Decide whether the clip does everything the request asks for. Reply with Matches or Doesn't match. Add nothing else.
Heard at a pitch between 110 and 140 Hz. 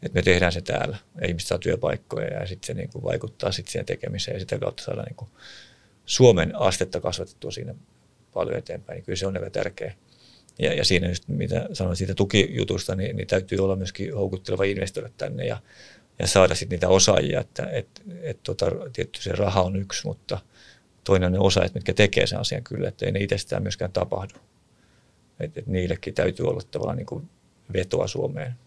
Doesn't match